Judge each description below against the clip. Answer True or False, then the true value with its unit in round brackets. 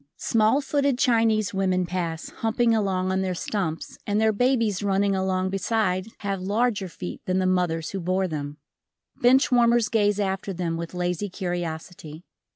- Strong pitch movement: False (3.4 semitones)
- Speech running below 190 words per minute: True (160 wpm)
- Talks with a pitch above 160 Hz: True (190 Hz)